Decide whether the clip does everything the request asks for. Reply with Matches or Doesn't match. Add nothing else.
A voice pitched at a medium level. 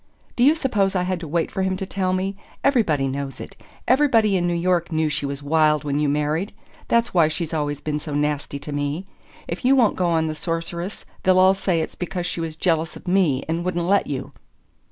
Matches